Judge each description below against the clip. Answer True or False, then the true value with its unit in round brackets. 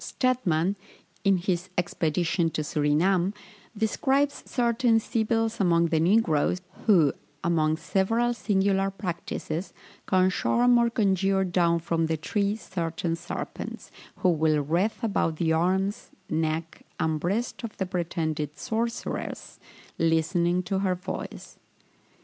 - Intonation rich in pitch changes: False (4.2 semitones)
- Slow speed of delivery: True (120 wpm)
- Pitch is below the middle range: False (180 Hz)